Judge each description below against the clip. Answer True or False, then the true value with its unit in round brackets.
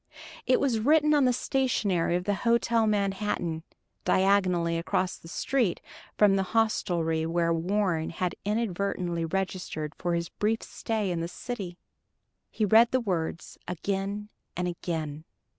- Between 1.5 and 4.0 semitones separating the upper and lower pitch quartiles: False (4.4 semitones)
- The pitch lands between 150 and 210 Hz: True (190 Hz)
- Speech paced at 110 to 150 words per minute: True (140 wpm)